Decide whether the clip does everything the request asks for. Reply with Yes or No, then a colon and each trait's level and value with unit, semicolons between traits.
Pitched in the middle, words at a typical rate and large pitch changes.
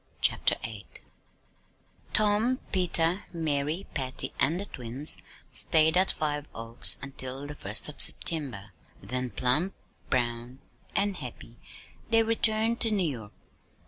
No: medium, 150 Hz; slow, 120 wpm; wide, 7.2 semitones